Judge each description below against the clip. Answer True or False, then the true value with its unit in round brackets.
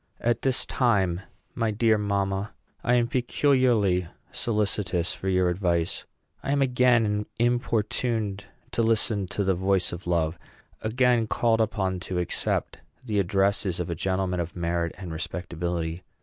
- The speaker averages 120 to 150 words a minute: True (140 wpm)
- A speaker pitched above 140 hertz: False (100 Hz)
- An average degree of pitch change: True (4.4 semitones)